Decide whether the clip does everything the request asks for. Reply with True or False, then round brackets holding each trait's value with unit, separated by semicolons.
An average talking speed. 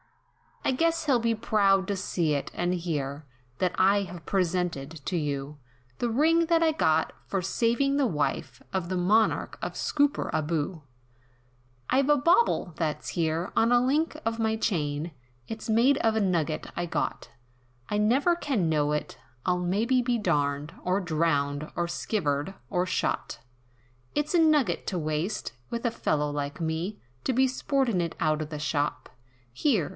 True (165 wpm)